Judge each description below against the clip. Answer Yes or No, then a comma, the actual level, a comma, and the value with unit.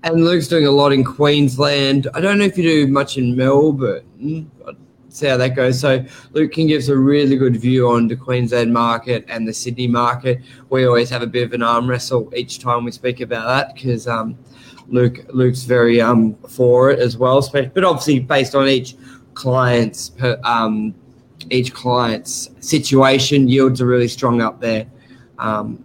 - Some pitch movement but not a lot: No, narrow, 2.0 semitones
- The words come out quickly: No, average, 185 wpm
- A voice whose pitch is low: Yes, low, 125 Hz